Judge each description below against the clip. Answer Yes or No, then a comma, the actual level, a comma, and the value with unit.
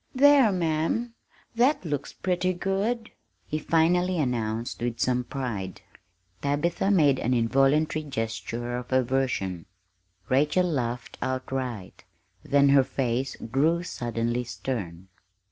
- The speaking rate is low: Yes, slow, 110 wpm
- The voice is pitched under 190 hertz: Yes, low, 135 Hz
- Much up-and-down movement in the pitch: Yes, wide, 6.0 semitones